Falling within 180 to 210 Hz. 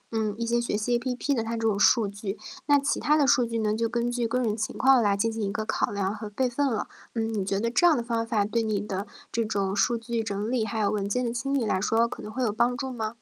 No: high, 225 Hz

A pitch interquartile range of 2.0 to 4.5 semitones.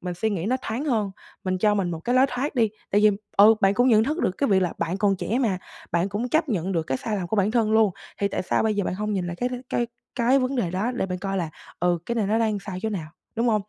Yes: average, 4.0 semitones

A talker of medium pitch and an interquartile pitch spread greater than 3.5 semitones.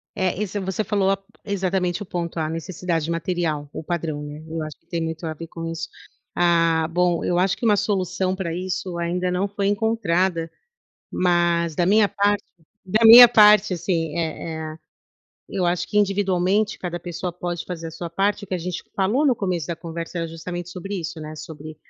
No: medium, 175 Hz; average, 2.7 semitones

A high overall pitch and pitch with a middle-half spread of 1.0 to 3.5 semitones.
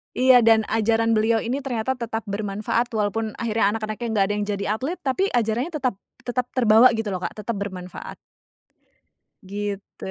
Yes: high, 225 Hz; average, 2.8 semitones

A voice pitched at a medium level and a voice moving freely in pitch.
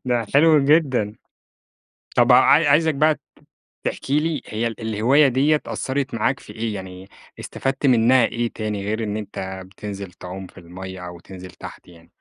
No: low, 110 Hz; wide, 6.3 semitones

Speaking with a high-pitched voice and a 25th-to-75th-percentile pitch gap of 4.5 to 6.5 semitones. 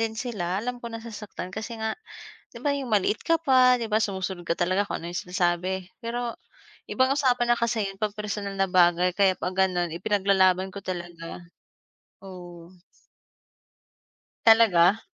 No: high, 200 Hz; average, 4.0 semitones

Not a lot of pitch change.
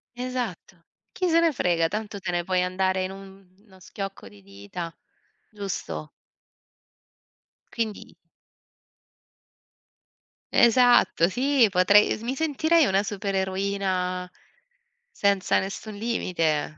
No: average, 3.8 semitones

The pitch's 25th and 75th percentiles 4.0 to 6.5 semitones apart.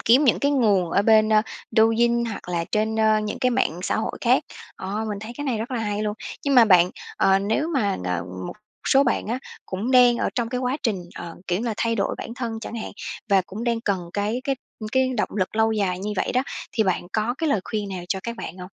No: average, 3.2 semitones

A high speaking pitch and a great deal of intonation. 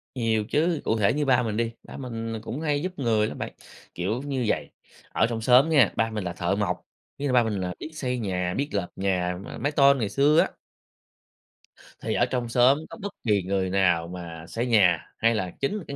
No: low, 115 Hz; wide, 6.1 semitones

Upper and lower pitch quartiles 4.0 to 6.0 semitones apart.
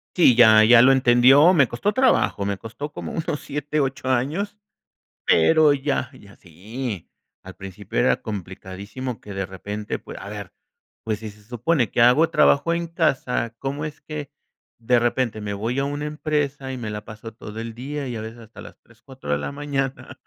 Yes: average, 5.2 semitones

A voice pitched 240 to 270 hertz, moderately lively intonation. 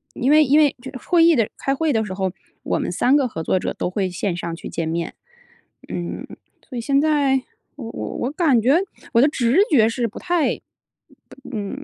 No: high, 245 Hz; wide, 6.5 semitones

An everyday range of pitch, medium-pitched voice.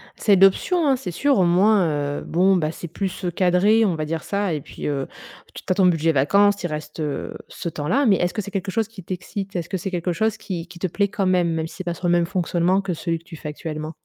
Yes: average, 3.3 semitones; medium, 180 Hz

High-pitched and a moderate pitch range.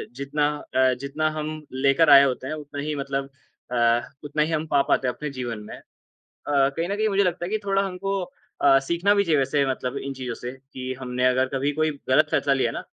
No: medium, 140 Hz; average, 3.0 semitones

